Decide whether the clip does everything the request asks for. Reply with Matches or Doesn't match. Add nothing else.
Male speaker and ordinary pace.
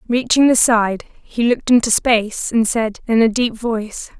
Doesn't match